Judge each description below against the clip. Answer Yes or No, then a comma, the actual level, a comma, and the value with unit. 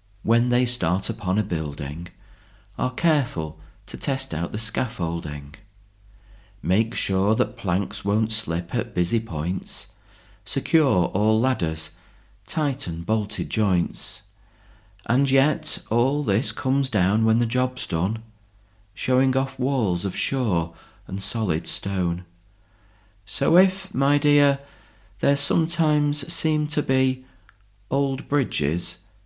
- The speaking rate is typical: No, slow, 115 wpm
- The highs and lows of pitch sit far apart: Yes, wide, 5.8 semitones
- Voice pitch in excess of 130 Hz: No, low, 105 Hz